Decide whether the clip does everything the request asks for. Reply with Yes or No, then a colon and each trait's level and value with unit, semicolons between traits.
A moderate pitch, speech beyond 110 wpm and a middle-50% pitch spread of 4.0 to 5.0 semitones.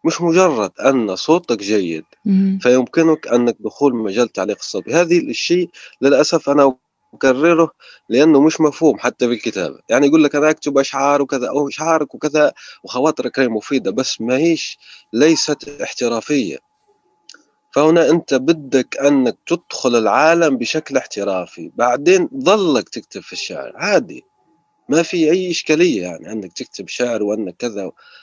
Yes: medium, 145 Hz; fast, 135 wpm; average, 4.4 semitones